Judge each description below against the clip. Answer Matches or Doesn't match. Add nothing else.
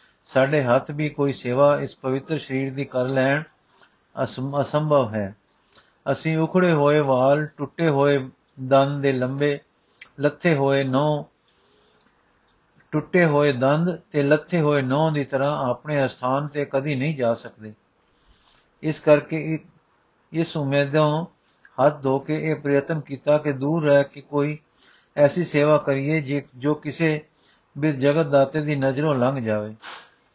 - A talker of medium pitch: Matches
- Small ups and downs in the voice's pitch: Matches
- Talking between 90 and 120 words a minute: Doesn't match